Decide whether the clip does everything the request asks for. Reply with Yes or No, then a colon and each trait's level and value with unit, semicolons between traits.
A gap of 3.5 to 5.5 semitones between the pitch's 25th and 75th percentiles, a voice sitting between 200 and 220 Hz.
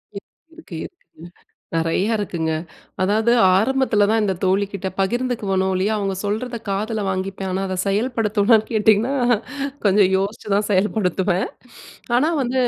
No: average, 2.9 semitones; high, 205 Hz